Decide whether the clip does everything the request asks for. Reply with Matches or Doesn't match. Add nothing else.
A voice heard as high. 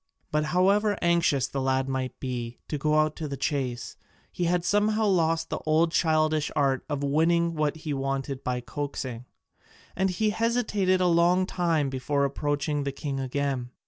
Doesn't match